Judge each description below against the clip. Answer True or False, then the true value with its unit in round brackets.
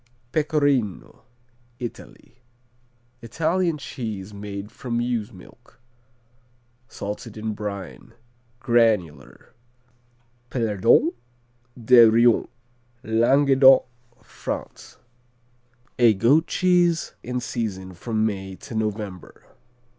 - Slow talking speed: True (80 wpm)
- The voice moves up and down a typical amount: True (3.8 semitones)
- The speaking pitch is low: True (115 Hz)